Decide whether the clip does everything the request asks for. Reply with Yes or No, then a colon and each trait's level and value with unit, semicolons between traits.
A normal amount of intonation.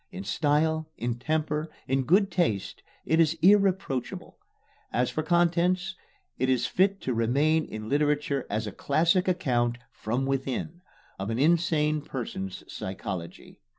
No: wide, 5.7 semitones